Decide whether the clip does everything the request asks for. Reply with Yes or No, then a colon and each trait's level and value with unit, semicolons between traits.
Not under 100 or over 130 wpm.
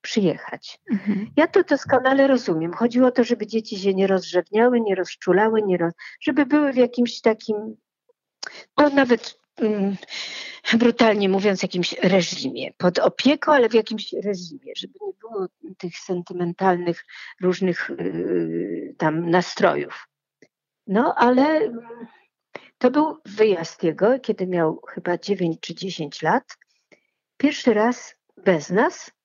Yes: average, 125 wpm